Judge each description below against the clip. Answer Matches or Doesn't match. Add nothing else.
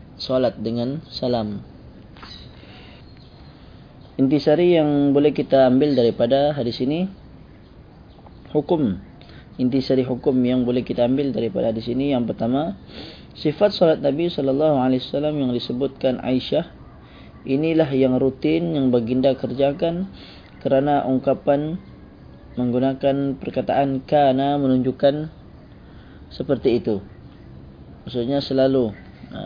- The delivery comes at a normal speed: Matches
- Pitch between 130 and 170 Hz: Matches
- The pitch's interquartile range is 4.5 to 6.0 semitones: Doesn't match